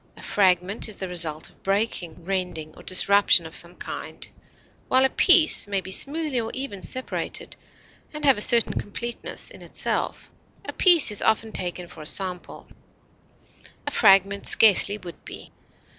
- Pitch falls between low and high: No, high, 200 Hz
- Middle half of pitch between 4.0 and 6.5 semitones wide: Yes, average, 4.8 semitones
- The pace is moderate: Yes, average, 160 wpm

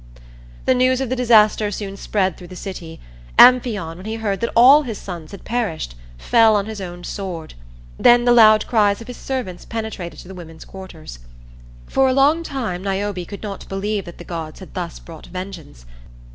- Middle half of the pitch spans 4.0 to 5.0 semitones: Yes, average, 4.7 semitones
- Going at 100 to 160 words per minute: No, average, 190 wpm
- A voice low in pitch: No, high, 200 Hz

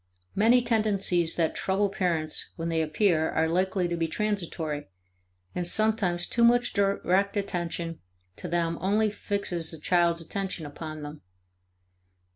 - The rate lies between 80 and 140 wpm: Yes, slow, 135 wpm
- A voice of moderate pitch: Yes, medium, 175 Hz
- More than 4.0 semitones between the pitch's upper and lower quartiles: No, average, 3.5 semitones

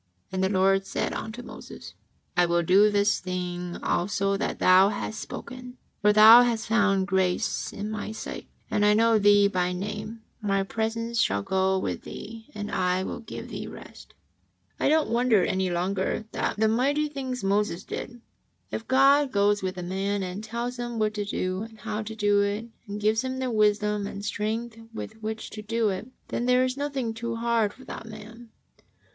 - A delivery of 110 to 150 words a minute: No, average, 190 wpm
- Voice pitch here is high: Yes, high, 210 Hz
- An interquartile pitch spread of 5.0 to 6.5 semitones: No, average, 3.0 semitones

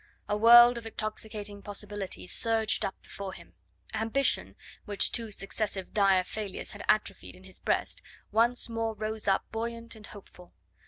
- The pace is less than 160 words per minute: Yes, average, 150 wpm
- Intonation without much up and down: Yes, narrow, 2.1 semitones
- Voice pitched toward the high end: Yes, high, 215 Hz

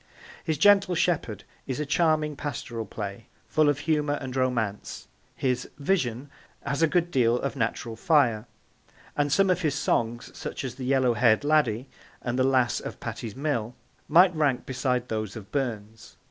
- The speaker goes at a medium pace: Yes, average, 165 wpm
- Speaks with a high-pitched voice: No, low, 130 Hz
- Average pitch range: Yes, average, 4.4 semitones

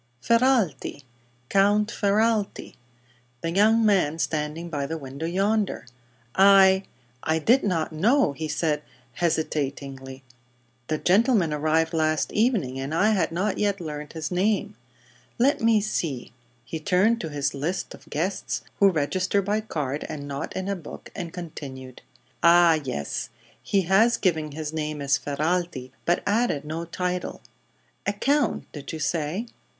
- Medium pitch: Yes, medium, 170 Hz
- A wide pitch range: No, average, 5.0 semitones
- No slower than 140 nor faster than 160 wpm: Yes, average, 145 wpm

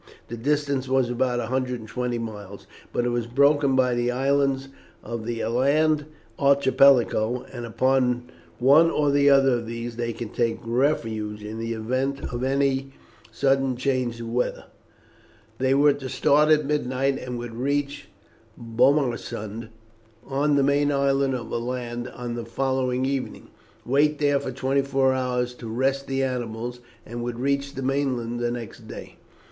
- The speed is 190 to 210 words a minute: No, average, 150 wpm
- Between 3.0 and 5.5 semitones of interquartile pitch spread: No, narrow, 2.5 semitones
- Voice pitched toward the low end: Yes, low, 130 Hz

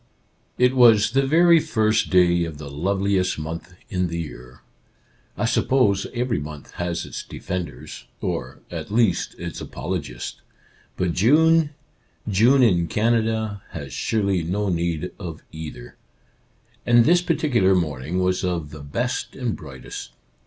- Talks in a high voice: No, very low, 95 Hz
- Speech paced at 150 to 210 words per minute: No, average, 140 wpm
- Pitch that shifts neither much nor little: No, wide, 5.9 semitones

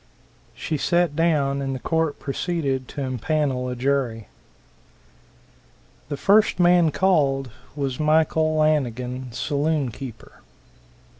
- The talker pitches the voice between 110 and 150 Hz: Yes, medium, 140 Hz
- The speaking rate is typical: No, slow, 105 wpm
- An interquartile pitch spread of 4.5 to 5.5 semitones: No, average, 3.3 semitones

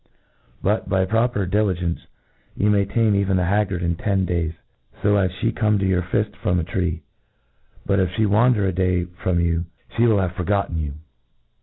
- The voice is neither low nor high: No, very low, 95 Hz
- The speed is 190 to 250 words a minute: Yes, average, 200 wpm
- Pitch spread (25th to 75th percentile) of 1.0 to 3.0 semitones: Yes, average, 2.7 semitones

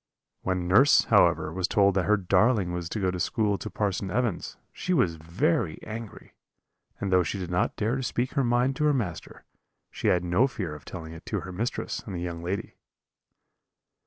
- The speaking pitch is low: Yes, very low, 95 Hz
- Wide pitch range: No, average, 4.5 semitones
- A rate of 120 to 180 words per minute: No, average, 200 wpm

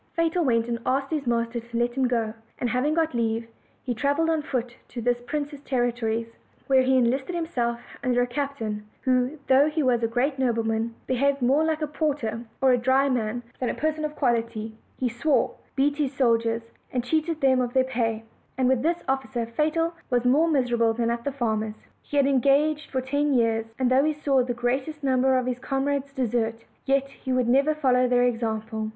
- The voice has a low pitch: No, very high, 255 Hz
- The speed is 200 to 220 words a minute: Yes, fast, 205 wpm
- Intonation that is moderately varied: Yes, average, 3.0 semitones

